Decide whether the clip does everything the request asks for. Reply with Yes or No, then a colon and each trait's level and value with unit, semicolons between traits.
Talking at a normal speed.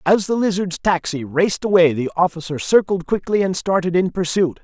Yes: average, 180 wpm